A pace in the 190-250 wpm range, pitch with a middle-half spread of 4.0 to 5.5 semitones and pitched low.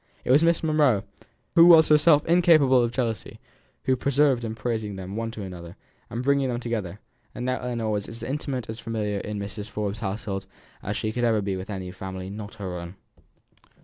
Yes: average, 200 wpm; average, 4.4 semitones; low, 115 Hz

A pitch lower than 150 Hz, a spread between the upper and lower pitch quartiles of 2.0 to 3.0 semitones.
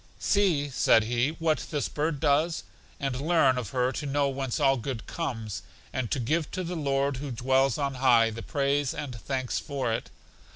Yes: low, 135 Hz; average, 2.7 semitones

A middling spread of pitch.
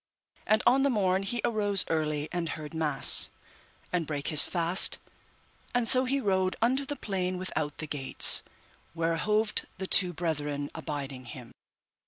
No: wide, 5.7 semitones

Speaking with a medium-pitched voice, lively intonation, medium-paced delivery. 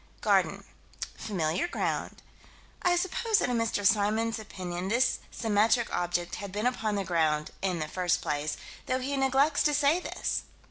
No: high, 215 Hz; wide, 6.6 semitones; average, 155 wpm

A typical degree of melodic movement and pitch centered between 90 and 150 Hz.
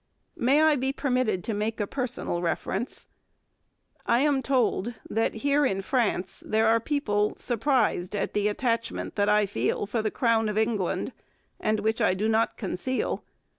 No: average, 3.5 semitones; high, 225 Hz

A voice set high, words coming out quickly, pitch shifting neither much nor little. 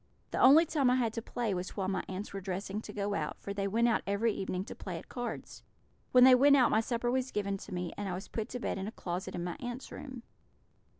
Yes: high, 210 Hz; fast, 270 wpm; average, 4.2 semitones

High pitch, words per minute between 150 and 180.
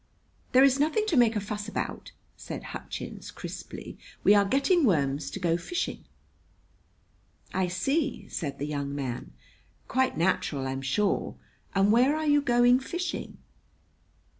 No: high, 210 Hz; average, 140 wpm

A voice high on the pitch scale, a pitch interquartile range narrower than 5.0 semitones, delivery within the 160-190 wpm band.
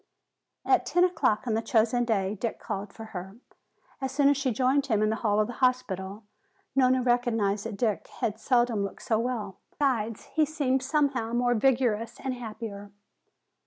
Yes: high, 235 Hz; average, 3.4 semitones; average, 175 wpm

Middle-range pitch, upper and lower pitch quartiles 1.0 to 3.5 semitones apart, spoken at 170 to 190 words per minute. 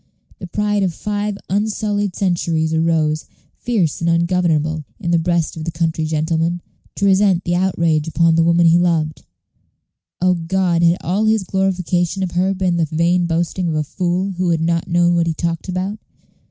Yes: medium, 175 Hz; narrow, 2.4 semitones; average, 180 wpm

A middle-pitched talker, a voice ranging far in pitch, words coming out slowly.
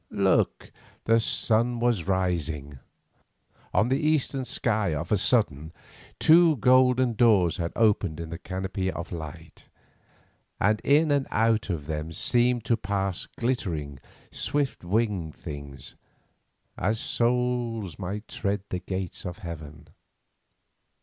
No: low, 100 Hz; wide, 6.1 semitones; slow, 125 wpm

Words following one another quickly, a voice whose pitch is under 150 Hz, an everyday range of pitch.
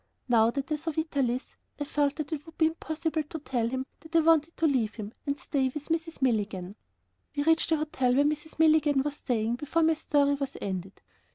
No: fast, 210 wpm; very high, 290 Hz; average, 3.9 semitones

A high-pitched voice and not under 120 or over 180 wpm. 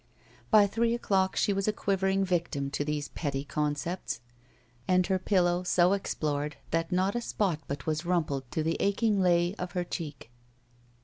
No: medium, 180 Hz; average, 170 wpm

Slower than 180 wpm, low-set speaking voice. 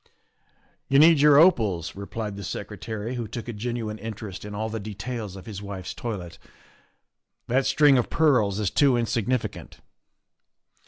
Yes: average, 170 wpm; low, 110 Hz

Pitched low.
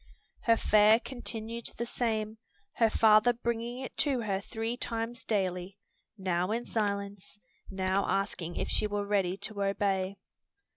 No: high, 215 Hz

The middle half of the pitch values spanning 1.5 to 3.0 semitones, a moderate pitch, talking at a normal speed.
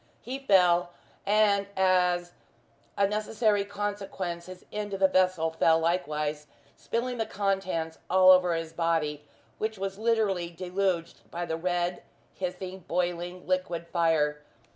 No: average, 2.7 semitones; medium, 180 Hz; slow, 130 wpm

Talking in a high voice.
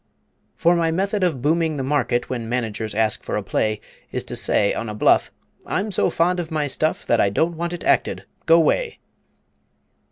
No: medium, 155 Hz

